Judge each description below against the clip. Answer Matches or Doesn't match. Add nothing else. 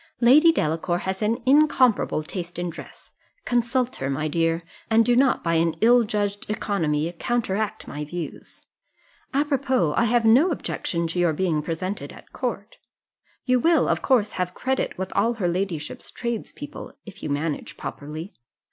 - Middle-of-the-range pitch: Doesn't match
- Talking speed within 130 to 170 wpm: Matches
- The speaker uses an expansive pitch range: Matches